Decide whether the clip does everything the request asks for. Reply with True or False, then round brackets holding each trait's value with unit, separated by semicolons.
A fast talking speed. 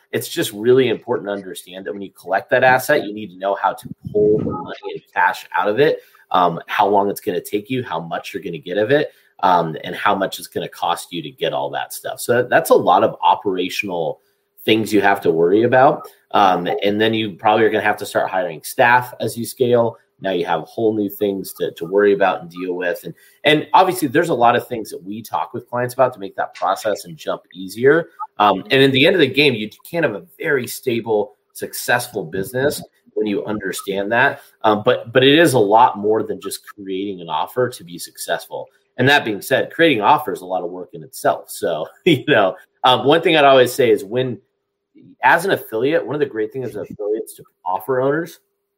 True (230 wpm)